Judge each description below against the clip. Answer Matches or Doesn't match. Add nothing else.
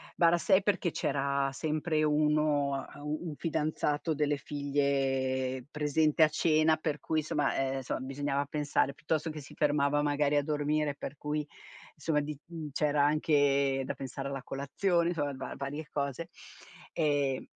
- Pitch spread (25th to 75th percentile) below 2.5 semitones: Matches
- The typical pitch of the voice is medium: Matches